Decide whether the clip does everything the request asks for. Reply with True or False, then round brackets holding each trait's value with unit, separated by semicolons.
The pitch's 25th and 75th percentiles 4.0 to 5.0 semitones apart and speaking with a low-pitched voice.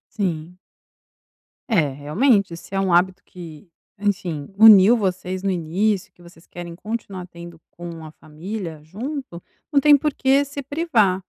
False (4.4 semitones; 185 Hz)